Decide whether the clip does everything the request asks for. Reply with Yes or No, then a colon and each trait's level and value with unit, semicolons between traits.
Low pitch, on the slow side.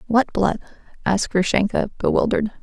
No: high, 210 Hz; slow, 115 wpm